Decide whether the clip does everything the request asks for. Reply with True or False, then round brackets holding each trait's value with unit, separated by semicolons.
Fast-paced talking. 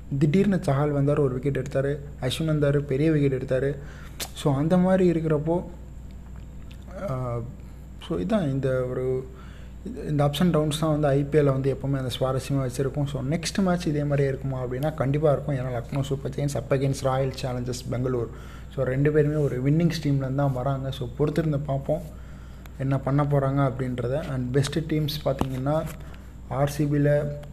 True (150 wpm)